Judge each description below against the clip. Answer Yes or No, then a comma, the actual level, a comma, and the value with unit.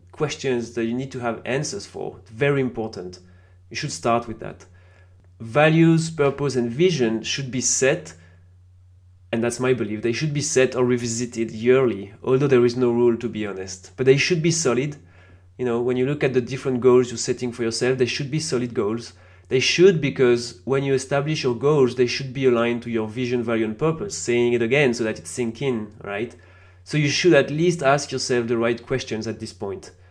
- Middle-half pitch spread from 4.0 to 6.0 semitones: No, average, 3.2 semitones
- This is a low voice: Yes, low, 120 Hz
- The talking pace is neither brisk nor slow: No, fast, 210 wpm